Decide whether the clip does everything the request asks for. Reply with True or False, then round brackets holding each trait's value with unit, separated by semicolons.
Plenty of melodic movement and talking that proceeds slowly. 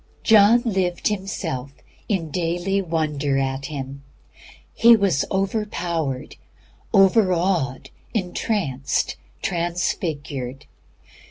True (5.8 semitones; 80 wpm)